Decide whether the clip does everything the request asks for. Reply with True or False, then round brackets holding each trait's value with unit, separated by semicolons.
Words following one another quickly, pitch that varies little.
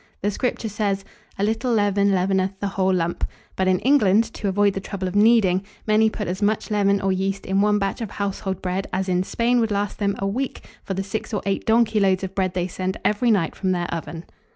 True (230 wpm; 1.9 semitones)